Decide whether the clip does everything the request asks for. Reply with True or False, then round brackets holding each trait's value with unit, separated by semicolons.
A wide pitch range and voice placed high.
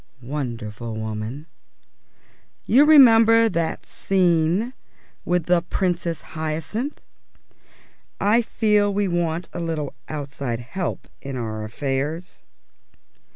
False (6.8 semitones; 165 Hz)